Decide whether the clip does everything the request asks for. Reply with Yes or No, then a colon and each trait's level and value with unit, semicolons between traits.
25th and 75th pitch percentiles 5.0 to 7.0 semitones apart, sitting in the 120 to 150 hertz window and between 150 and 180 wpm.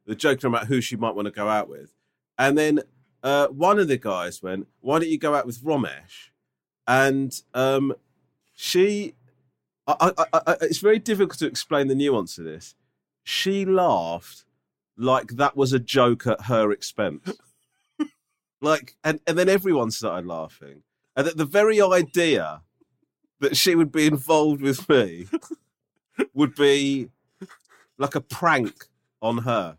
Yes: wide, 5.5 semitones; medium, 140 Hz; average, 155 wpm